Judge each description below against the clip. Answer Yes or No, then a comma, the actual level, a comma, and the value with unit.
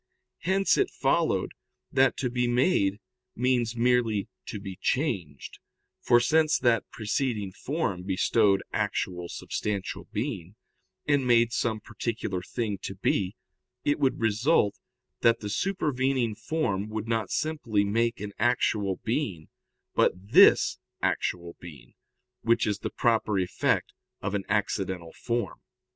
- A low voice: Yes, low, 110 Hz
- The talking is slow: Yes, slow, 125 wpm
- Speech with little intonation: No, average, 3.9 semitones